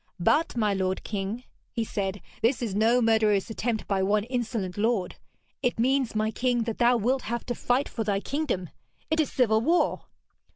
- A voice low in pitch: No, high, 225 Hz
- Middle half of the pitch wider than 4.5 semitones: No, average, 3.1 semitones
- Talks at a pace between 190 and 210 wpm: No, average, 180 wpm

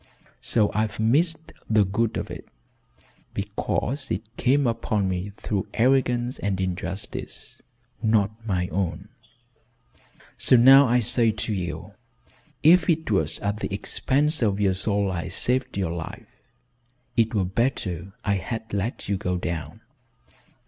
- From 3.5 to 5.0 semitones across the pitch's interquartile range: Yes, average, 4.2 semitones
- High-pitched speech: No, low, 105 Hz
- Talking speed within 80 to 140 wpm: Yes, slow, 135 wpm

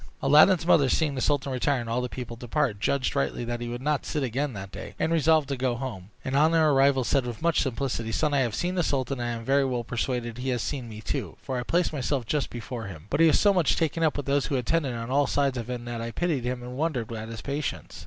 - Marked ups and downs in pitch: No, average, 3.5 semitones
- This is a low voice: Yes, low, 130 Hz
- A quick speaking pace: Yes, fast, 270 wpm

